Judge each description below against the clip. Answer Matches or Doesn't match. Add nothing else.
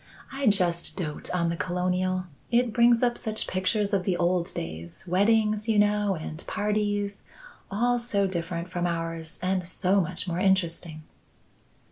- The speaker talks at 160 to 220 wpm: Doesn't match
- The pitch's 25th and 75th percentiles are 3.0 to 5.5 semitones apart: Matches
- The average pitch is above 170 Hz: Matches